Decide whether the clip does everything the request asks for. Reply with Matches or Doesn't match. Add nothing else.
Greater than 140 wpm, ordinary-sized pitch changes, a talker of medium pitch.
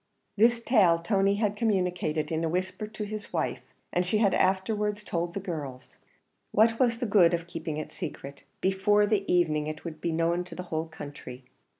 Matches